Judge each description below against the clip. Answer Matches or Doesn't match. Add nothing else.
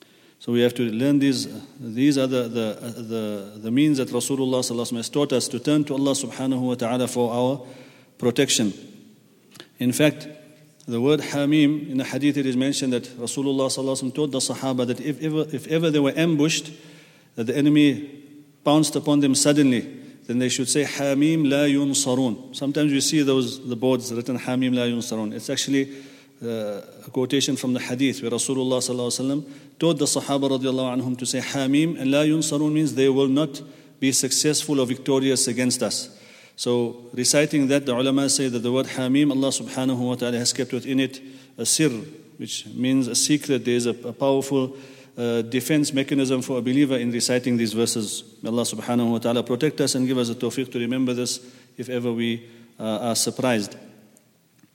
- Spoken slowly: Doesn't match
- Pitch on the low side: Matches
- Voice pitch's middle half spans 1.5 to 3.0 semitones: Matches